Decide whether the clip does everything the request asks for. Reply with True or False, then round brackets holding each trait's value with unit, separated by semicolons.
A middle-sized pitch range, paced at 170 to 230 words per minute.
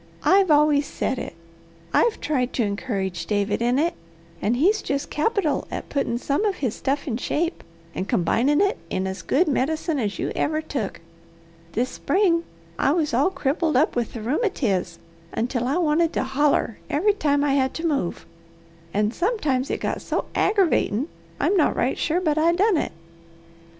False (5.7 semitones; 175 wpm)